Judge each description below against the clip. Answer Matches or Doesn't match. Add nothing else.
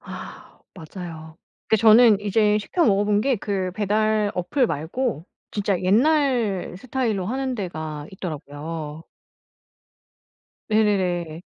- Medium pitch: Doesn't match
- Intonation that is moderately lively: Matches